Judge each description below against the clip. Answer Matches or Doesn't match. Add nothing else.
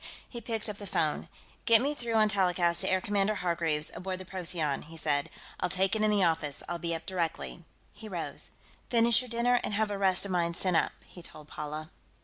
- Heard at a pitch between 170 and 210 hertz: Matches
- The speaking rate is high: Matches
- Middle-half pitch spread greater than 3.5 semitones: Matches